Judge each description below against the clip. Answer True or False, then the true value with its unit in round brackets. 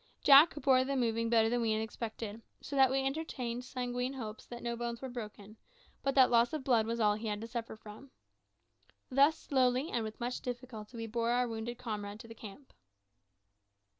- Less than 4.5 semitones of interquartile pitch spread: True (2.6 semitones)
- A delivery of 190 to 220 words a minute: True (195 wpm)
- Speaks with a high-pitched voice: True (240 Hz)